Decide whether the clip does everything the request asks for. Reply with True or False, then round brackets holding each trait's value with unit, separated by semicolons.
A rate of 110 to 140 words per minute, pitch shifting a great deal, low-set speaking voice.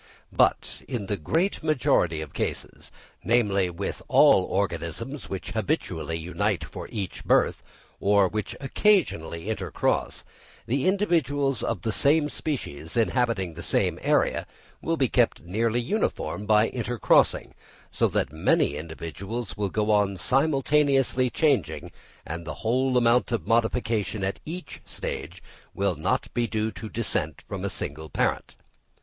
True (135 wpm; 6.5 semitones; 110 Hz)